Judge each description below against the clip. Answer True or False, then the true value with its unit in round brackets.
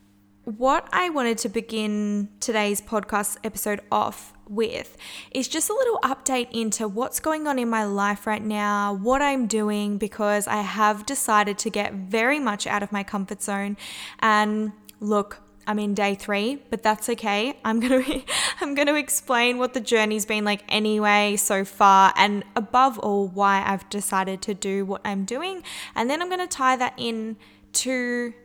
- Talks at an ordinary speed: True (170 wpm)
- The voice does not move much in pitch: False (3.4 semitones)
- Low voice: False (215 Hz)